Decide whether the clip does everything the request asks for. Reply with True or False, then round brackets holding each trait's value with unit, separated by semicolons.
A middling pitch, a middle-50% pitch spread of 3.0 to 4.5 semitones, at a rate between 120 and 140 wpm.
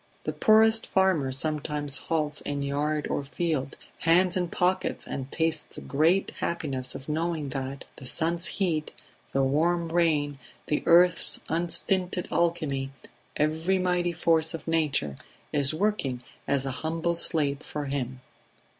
True (155 Hz; 3.4 semitones; 135 wpm)